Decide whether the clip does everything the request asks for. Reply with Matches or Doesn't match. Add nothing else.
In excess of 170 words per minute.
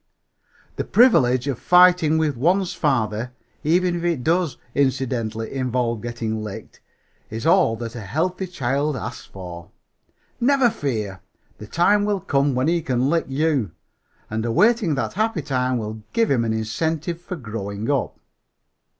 Doesn't match